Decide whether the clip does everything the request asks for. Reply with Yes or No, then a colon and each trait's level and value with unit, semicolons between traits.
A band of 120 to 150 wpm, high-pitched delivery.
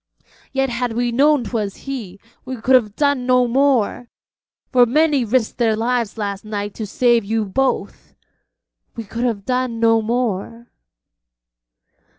Yes: average, 145 wpm; high, 235 Hz